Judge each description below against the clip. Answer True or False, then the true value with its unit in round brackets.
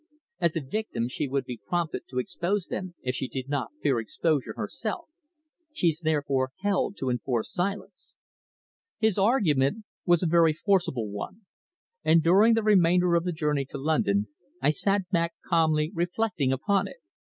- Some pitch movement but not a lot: False (6.0 semitones)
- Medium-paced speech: True (160 wpm)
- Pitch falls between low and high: True (165 Hz)